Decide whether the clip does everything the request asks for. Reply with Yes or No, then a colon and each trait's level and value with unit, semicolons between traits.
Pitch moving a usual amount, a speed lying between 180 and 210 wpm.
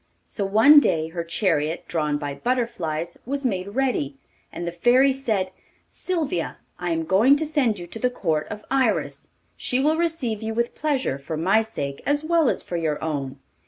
No: wide, 8.5 semitones; average, 185 wpm